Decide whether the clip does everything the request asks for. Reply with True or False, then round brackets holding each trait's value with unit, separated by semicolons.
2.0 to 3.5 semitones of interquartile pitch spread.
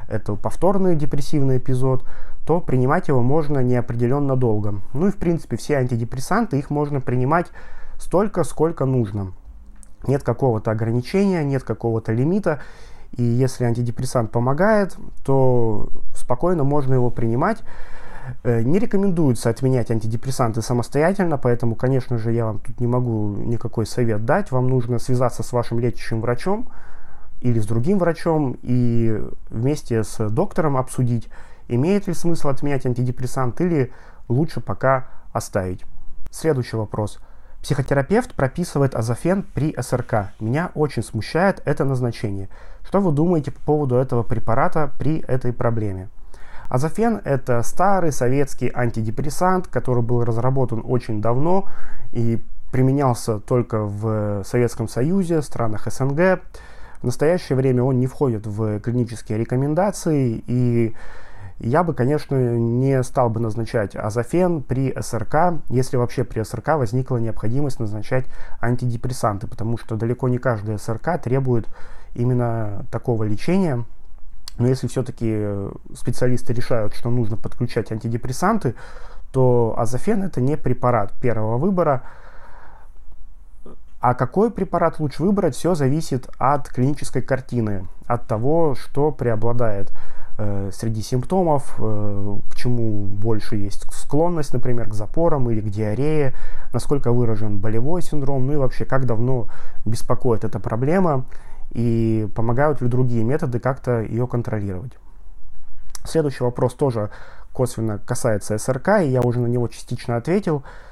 False (3.9 semitones)